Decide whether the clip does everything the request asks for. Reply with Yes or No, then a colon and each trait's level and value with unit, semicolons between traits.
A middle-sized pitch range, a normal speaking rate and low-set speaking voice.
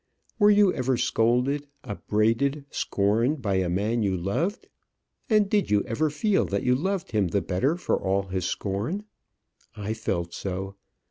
No: wide, 7.2 semitones; average, 155 wpm; low, 115 Hz